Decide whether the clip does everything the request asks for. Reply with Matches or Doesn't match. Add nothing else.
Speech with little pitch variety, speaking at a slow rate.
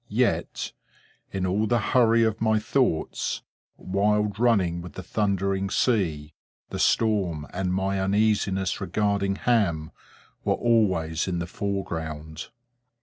Doesn't match